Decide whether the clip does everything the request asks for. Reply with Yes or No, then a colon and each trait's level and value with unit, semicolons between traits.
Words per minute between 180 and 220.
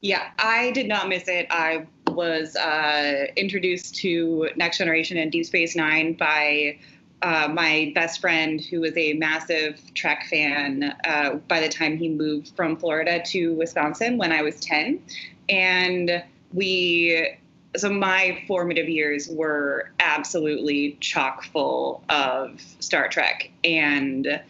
No: slow, 135 wpm